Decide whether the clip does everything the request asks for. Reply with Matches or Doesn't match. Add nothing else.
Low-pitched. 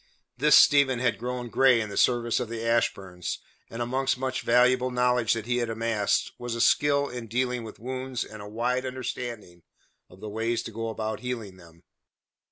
Matches